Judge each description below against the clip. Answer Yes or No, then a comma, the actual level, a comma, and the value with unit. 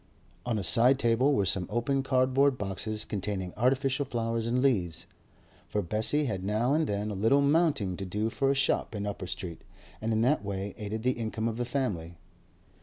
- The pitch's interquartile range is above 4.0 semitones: Yes, average, 4.5 semitones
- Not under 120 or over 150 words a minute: No, average, 190 wpm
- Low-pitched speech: Yes, low, 115 Hz